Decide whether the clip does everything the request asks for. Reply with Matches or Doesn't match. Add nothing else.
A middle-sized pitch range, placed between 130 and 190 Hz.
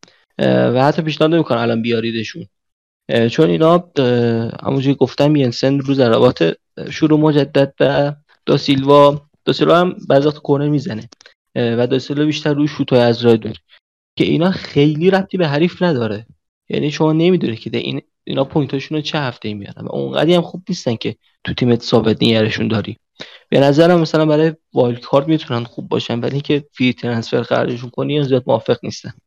Matches